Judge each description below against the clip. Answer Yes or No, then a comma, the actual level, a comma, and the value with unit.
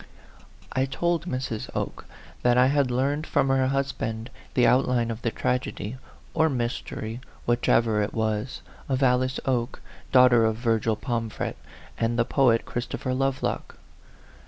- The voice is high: No, low, 125 Hz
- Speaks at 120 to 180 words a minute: Yes, slow, 135 wpm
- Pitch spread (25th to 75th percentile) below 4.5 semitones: Yes, narrow, 2.6 semitones